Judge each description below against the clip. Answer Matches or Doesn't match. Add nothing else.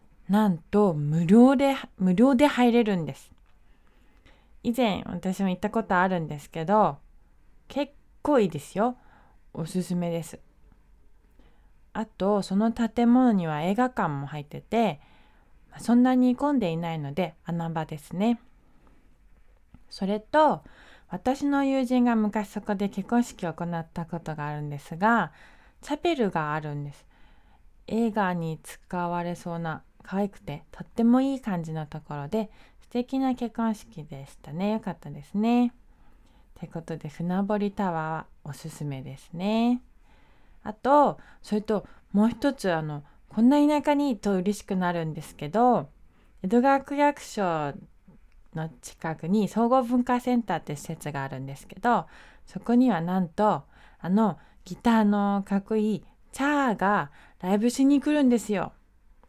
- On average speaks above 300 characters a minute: Doesn't match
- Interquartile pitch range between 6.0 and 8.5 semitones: Matches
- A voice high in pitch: Matches